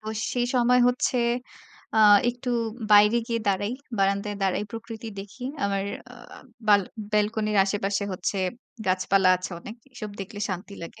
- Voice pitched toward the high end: Yes, high, 205 Hz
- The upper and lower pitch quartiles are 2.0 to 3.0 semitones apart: Yes, narrow, 2.6 semitones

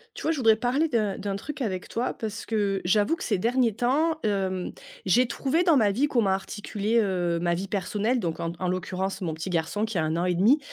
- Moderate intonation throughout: Yes, average, 4.7 semitones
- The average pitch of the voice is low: No, high, 205 Hz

